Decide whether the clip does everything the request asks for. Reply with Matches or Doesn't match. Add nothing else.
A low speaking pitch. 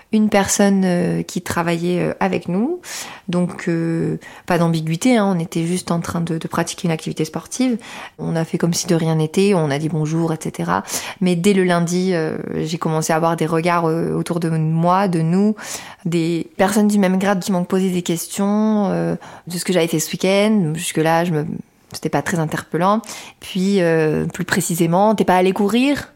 Doesn't match